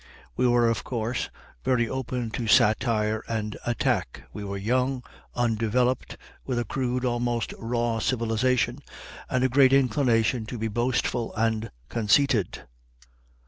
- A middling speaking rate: No, slow, 130 wpm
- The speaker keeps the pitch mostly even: Yes, narrow, 2.2 semitones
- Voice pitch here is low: Yes, low, 120 Hz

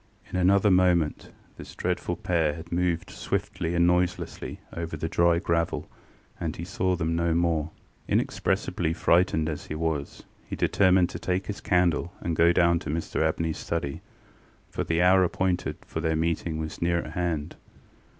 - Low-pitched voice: Yes, very low, 85 Hz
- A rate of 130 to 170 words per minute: Yes, average, 165 wpm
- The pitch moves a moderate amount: No, narrow, 1.7 semitones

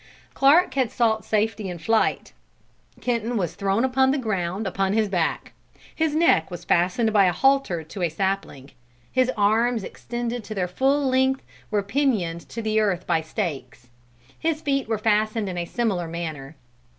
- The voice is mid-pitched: No, high, 215 Hz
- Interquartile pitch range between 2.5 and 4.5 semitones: No, wide, 5.5 semitones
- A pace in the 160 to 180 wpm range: Yes, average, 165 wpm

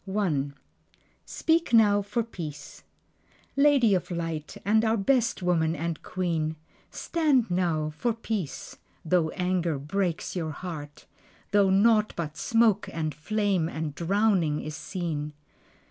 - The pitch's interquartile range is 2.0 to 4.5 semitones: No, average, 5.3 semitones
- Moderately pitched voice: Yes, medium, 180 Hz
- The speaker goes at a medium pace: No, slow, 120 wpm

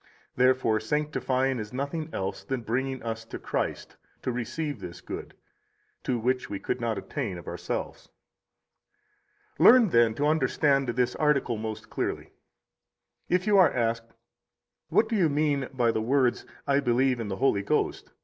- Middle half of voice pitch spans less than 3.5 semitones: No, average, 3.9 semitones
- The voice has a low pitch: Yes, low, 130 Hz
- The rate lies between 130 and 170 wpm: Yes, average, 160 wpm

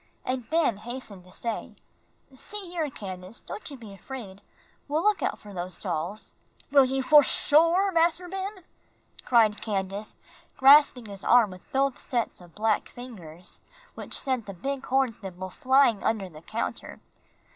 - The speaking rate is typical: Yes, average, 155 wpm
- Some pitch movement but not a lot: No, wide, 6.1 semitones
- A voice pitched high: Yes, high, 240 Hz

